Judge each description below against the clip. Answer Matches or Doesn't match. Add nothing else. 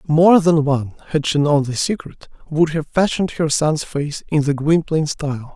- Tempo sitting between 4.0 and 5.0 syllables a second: Matches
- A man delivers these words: Matches